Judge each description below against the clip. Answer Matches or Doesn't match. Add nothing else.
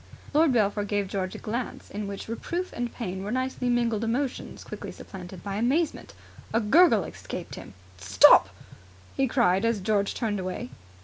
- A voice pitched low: Doesn't match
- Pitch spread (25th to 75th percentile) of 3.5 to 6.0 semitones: Matches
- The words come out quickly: Doesn't match